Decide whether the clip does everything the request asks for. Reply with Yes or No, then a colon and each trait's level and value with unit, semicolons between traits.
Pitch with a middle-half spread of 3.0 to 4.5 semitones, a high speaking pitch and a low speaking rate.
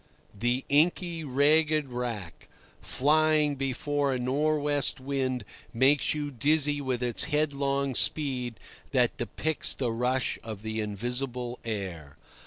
No: average, 3.3 semitones; low, 135 Hz; slow, 120 wpm